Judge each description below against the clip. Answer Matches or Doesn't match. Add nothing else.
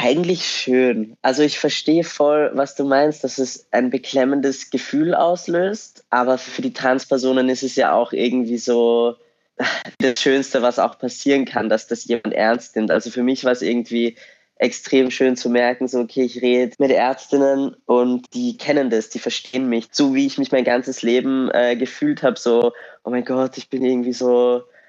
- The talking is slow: Doesn't match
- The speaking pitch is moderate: Doesn't match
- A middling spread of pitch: Doesn't match